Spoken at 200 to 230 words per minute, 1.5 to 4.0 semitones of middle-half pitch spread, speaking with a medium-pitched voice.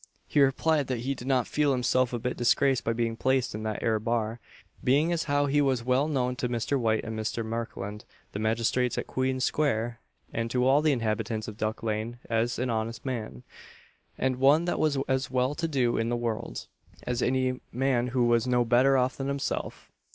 No: fast, 205 wpm; average, 2.7 semitones; low, 125 Hz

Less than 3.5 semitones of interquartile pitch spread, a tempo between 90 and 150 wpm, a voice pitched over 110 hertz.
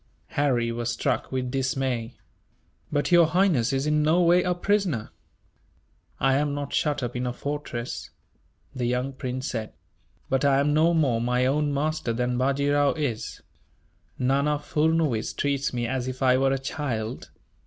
No: average, 3.1 semitones; average, 165 wpm; low, 135 Hz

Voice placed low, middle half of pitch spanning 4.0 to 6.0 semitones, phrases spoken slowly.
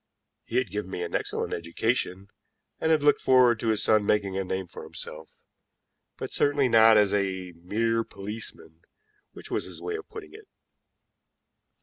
No: low, 105 Hz; average, 4.7 semitones; average, 165 wpm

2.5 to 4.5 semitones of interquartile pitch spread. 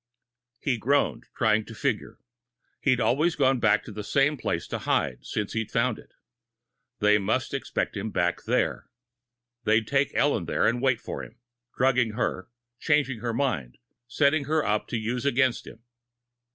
Yes: average, 4.1 semitones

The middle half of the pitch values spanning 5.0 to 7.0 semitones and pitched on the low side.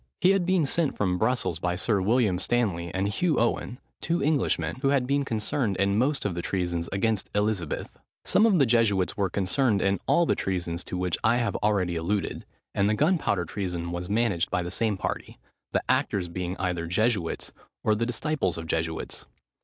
Yes: wide, 5.4 semitones; low, 100 Hz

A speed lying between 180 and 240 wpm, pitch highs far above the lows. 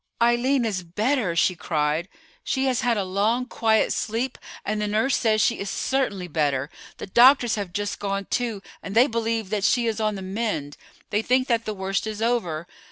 No: average, 195 wpm; average, 3.7 semitones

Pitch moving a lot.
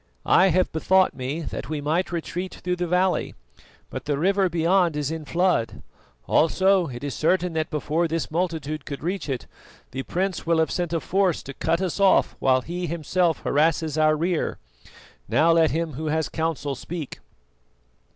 No: average, 2.8 semitones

